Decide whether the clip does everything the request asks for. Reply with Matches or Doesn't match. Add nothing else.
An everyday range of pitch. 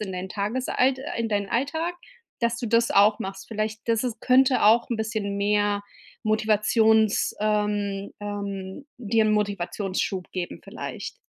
Doesn't match